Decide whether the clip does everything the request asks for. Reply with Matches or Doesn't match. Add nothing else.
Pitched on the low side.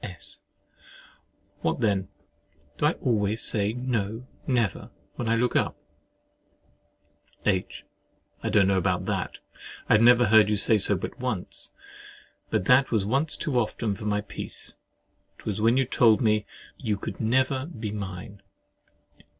Matches